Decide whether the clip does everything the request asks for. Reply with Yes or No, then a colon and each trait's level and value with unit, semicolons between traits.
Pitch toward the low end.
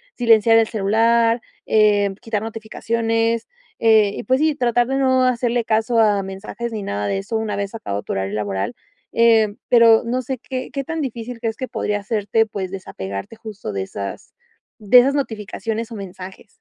No: high, 225 Hz